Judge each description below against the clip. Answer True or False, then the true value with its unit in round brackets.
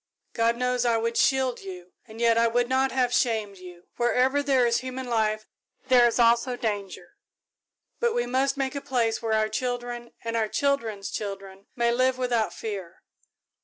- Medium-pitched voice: False (235 Hz)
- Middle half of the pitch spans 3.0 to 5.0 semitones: False (2.6 semitones)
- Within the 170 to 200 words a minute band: True (175 wpm)